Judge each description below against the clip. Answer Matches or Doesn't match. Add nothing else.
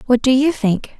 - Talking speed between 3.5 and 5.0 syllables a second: Matches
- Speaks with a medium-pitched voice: Doesn't match